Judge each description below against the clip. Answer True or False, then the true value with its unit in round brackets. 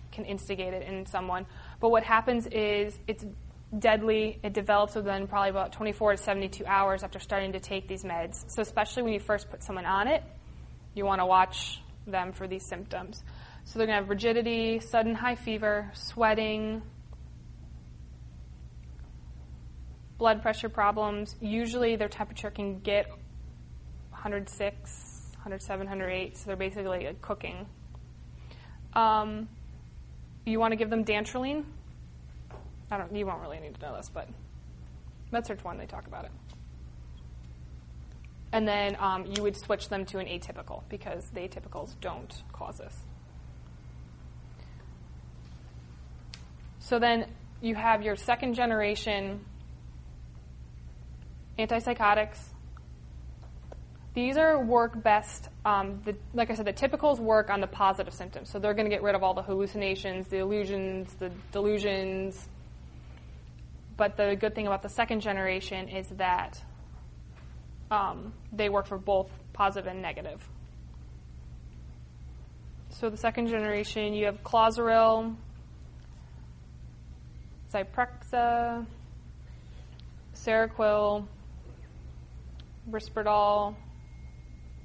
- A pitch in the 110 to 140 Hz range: False (190 Hz)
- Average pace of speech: False (125 wpm)